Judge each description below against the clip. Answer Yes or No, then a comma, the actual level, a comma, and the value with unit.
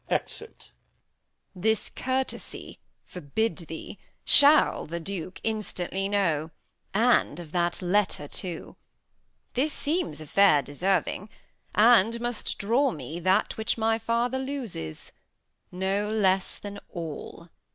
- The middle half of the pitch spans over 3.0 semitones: Yes, average, 4.9 semitones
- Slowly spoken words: Yes, slow, 115 wpm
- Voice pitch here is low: No, high, 200 Hz